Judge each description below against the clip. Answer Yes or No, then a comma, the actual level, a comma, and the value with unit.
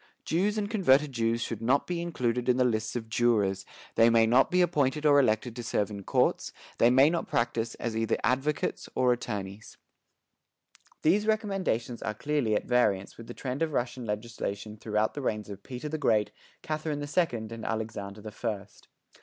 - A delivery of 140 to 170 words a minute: No, average, 185 wpm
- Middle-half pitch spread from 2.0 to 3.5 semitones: No, average, 4.9 semitones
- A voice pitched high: No, low, 120 Hz